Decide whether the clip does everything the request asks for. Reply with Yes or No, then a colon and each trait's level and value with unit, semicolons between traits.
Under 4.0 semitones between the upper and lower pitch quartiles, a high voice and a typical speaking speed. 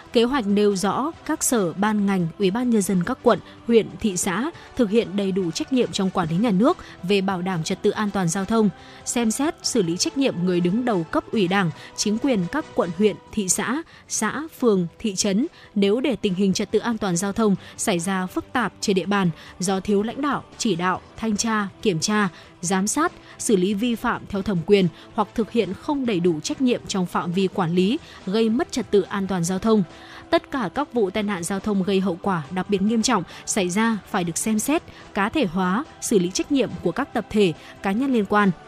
Yes: average, 3.6 semitones; high, 205 Hz; average, 235 wpm